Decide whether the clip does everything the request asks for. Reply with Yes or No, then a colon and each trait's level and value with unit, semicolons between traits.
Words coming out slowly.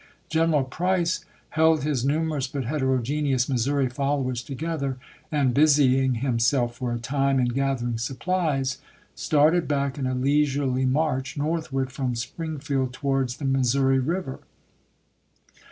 Yes: slow, 125 wpm